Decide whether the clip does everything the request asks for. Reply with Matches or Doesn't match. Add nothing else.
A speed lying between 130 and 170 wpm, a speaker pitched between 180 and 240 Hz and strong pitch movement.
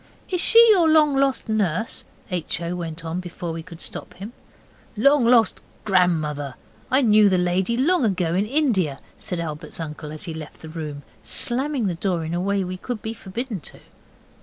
Doesn't match